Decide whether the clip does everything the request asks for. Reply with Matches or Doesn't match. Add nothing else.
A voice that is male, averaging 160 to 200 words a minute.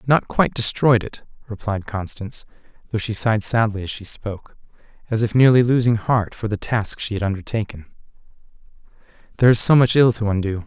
Matches